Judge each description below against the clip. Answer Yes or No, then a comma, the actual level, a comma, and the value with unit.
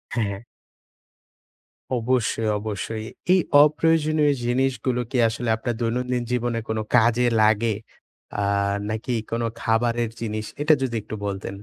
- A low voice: Yes, low, 120 Hz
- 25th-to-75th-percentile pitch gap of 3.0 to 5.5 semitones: No, narrow, 2.4 semitones